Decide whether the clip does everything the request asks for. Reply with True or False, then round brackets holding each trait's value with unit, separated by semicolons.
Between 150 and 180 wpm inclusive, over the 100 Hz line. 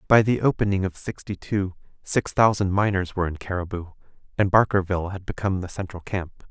False (175 wpm; 95 Hz)